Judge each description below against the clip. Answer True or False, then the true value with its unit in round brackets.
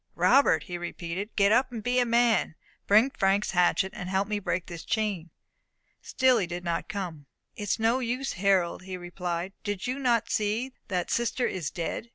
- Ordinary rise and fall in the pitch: True (4.7 semitones)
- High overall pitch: True (200 Hz)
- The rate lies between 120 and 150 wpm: False (190 wpm)